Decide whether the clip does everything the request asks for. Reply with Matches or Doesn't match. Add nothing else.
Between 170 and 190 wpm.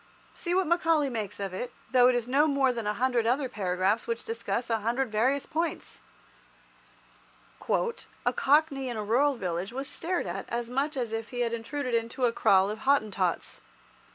Matches